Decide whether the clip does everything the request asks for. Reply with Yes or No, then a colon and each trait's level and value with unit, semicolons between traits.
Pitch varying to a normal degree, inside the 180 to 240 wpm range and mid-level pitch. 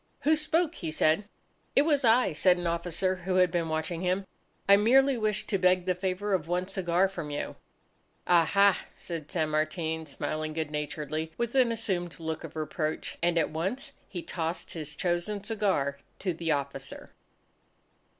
No: average, 3.9 semitones; average, 170 wpm; medium, 175 Hz